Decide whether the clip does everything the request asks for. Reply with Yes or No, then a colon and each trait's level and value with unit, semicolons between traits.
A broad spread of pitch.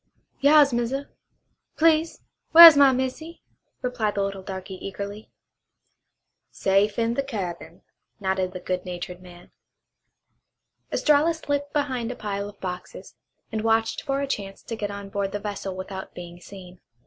Yes: wide, 6.2 semitones